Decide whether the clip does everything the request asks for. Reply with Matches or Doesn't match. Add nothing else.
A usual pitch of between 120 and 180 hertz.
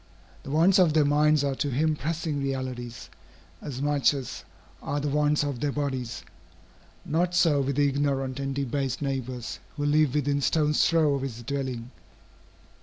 Matches